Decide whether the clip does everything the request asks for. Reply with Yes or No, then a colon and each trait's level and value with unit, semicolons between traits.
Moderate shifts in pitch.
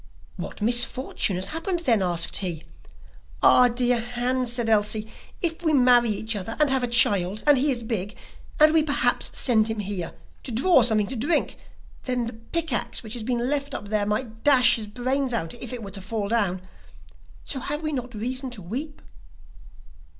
Yes: average, 3.7 semitones